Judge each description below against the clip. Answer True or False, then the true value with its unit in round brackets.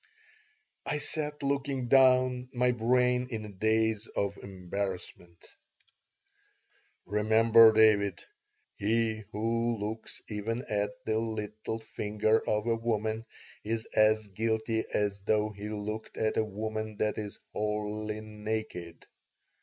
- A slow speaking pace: True (115 wpm)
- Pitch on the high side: False (110 Hz)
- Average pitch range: False (1.5 semitones)